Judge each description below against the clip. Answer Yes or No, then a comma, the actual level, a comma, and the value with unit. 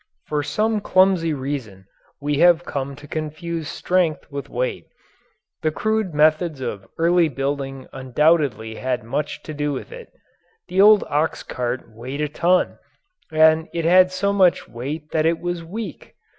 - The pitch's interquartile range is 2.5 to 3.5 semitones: No, average, 4.2 semitones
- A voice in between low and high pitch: Yes, medium, 155 Hz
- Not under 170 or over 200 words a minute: No, average, 155 wpm